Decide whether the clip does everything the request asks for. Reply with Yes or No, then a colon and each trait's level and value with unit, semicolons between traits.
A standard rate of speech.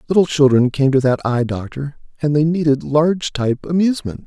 Yes: average, 185 wpm